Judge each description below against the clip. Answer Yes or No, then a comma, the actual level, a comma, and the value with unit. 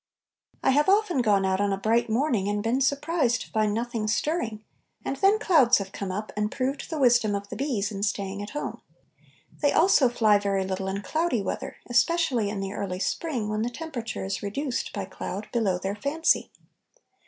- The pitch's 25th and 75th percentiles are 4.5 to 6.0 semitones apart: Yes, wide, 5.4 semitones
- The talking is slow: No, average, 195 wpm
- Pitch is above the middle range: Yes, high, 225 Hz